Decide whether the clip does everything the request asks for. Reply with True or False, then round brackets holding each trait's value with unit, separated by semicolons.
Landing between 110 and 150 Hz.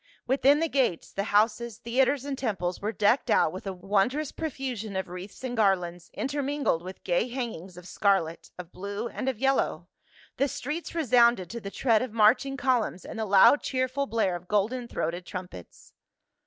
False (220 Hz)